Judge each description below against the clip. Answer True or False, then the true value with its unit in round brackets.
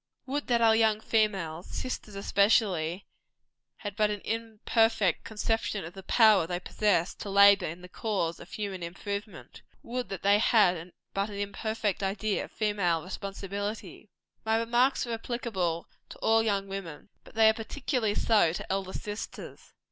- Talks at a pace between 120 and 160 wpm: True (155 wpm)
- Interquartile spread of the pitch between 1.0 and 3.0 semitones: True (2.7 semitones)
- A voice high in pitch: True (205 Hz)